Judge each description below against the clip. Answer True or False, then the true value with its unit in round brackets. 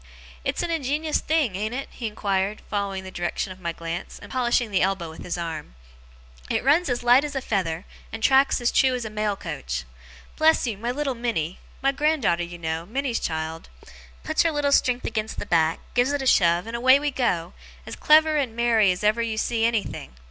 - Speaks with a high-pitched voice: True (225 Hz)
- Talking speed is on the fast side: True (215 wpm)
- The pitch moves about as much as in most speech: False (6.8 semitones)